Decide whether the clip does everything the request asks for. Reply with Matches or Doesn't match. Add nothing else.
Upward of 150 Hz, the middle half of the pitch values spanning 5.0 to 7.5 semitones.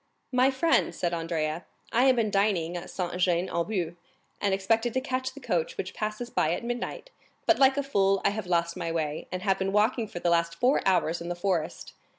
Matches